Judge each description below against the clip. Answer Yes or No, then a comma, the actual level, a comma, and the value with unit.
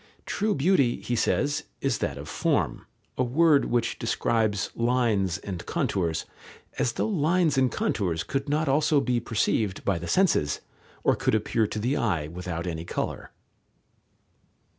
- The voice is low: Yes, low, 120 Hz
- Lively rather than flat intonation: Yes, wide, 6.9 semitones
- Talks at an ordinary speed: Yes, average, 150 wpm